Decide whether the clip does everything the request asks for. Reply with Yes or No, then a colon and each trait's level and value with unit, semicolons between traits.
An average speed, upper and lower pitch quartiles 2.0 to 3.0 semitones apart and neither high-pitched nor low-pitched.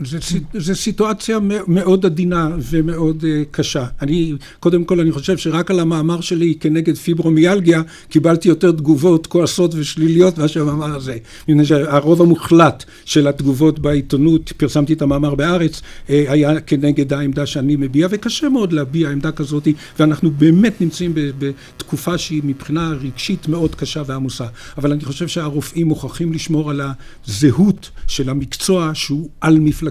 Yes: average, 140 wpm; narrow, 2.6 semitones; medium, 155 Hz